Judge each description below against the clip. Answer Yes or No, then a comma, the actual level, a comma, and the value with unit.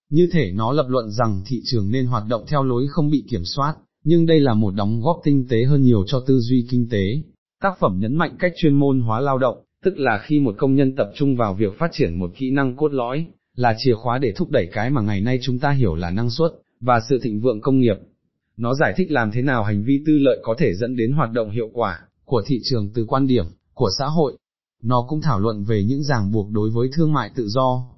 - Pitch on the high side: No, low, 125 Hz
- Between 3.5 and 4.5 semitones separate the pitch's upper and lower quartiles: Yes, average, 4.1 semitones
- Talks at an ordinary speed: No, fast, 260 wpm